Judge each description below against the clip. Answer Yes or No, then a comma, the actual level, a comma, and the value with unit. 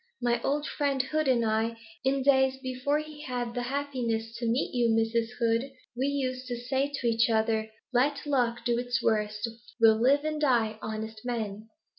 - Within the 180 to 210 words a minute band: Yes, average, 185 wpm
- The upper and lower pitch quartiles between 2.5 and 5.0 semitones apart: Yes, average, 3.1 semitones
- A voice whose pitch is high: Yes, high, 245 Hz